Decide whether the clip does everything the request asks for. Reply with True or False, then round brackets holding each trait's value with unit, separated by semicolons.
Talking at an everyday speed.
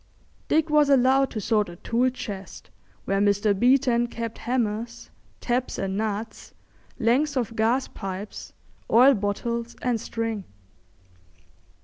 False (120 wpm)